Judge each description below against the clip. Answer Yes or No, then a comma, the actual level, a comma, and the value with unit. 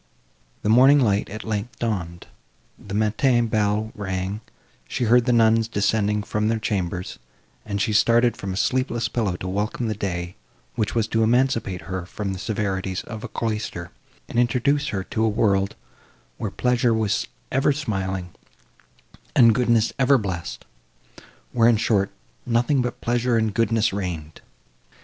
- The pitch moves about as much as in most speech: Yes, average, 3.4 semitones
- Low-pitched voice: Yes, low, 110 Hz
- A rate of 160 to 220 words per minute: No, average, 150 wpm